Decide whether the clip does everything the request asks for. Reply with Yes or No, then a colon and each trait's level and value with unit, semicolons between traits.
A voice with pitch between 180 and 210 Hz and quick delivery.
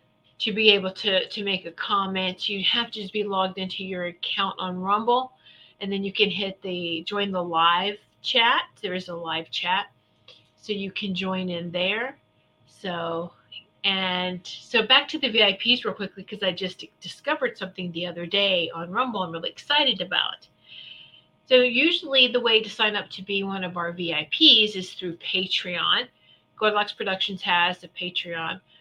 No: high, 190 Hz; average, 175 wpm